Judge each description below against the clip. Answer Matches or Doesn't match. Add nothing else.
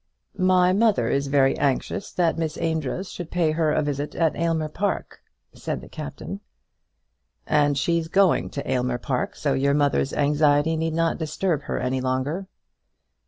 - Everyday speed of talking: Matches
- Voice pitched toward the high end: Doesn't match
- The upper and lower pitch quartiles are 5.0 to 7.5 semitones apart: Doesn't match